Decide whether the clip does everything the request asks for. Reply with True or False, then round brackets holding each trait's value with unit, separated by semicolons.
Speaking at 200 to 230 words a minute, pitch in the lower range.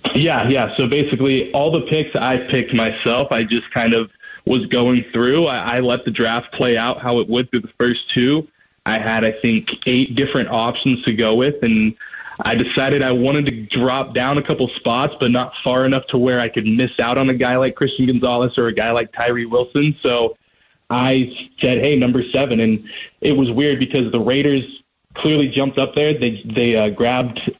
True (205 wpm; 125 Hz)